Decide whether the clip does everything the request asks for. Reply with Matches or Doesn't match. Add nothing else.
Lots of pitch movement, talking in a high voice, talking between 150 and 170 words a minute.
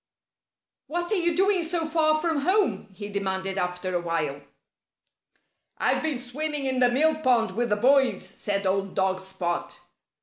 Matches